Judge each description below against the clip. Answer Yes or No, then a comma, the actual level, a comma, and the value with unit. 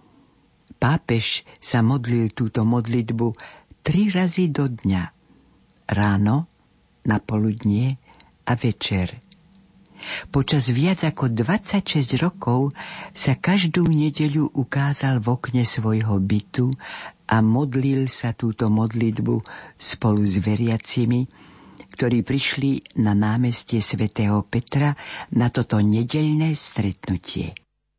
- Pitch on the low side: Yes, low, 125 Hz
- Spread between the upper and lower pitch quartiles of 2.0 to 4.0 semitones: No, average, 4.5 semitones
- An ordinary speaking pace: No, slow, 95 wpm